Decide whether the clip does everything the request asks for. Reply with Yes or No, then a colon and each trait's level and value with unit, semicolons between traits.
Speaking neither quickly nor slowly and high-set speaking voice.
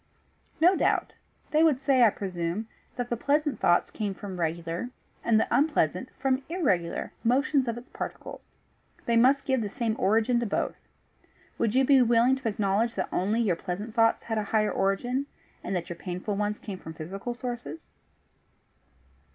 Yes: average, 170 wpm; high, 225 Hz